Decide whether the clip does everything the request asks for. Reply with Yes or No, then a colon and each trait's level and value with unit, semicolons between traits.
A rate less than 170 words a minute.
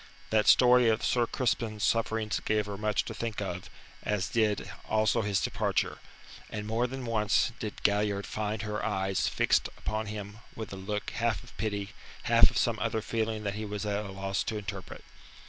No: average, 185 wpm